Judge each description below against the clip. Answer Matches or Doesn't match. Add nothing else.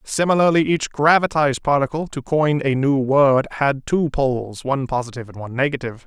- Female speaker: Doesn't match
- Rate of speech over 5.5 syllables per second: Matches